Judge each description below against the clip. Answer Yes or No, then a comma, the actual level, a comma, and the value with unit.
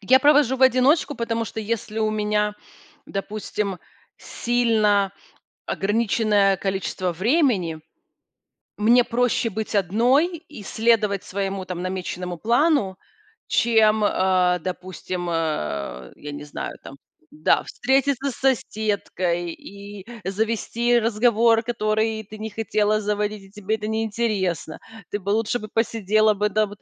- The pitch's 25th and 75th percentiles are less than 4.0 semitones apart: Yes, average, 3.1 semitones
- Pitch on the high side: Yes, high, 215 Hz